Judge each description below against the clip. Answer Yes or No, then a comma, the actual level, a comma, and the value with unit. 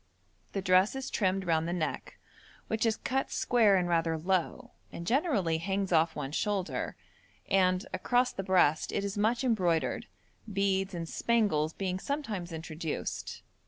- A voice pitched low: No, high, 190 Hz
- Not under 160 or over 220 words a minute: No, average, 150 wpm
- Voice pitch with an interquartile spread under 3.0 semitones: No, average, 4.2 semitones